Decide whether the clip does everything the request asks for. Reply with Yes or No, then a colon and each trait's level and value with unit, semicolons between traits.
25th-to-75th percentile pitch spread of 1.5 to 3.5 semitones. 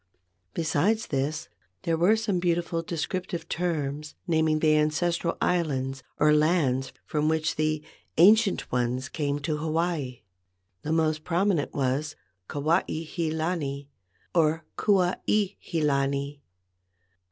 Yes: average, 3.0 semitones